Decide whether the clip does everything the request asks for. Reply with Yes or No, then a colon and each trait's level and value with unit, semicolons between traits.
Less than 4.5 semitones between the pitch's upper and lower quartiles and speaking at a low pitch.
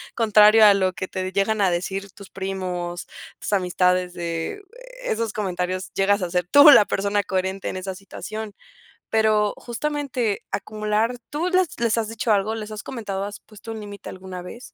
No: average, 2.8 semitones; high, 205 Hz